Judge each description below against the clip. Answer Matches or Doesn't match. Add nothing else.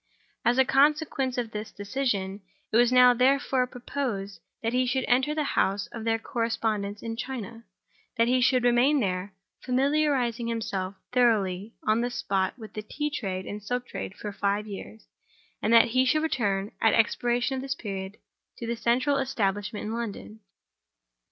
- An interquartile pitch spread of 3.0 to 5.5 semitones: Matches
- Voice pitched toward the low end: Doesn't match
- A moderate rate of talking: Matches